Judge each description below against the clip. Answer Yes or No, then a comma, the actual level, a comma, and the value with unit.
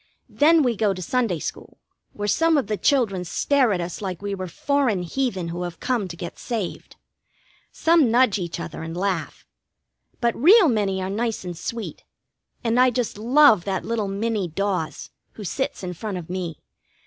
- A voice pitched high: Yes, high, 205 Hz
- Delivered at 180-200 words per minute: Yes, average, 185 wpm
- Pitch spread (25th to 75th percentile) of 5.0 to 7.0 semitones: Yes, average, 5.3 semitones